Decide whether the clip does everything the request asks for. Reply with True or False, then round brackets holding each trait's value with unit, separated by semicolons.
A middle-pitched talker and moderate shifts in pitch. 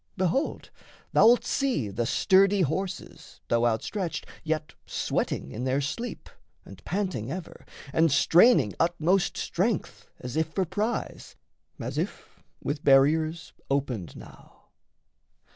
False (160 Hz; 6.0 semitones)